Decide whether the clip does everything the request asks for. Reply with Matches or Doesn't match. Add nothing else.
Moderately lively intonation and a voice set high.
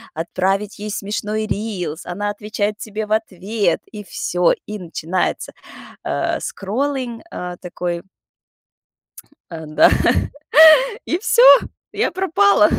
Matches